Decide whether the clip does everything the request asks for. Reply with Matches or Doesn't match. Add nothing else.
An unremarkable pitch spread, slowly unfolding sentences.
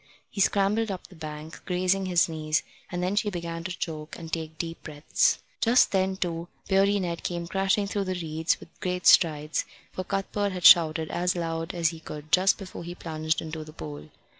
Doesn't match